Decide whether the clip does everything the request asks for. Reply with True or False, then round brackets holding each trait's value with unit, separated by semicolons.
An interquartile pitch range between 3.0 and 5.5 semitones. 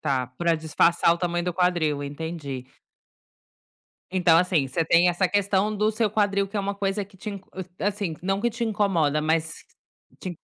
True (3.8 semitones)